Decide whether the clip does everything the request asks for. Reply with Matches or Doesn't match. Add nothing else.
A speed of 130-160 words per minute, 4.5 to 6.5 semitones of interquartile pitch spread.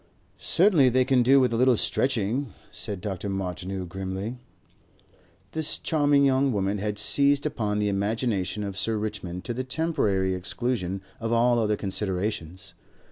Matches